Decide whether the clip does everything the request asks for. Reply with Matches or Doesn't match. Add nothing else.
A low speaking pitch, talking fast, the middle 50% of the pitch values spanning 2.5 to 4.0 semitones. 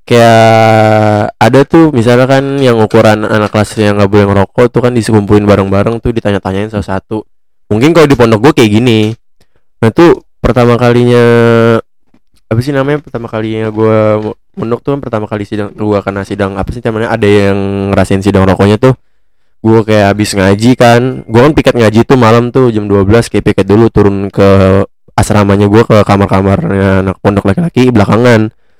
Matches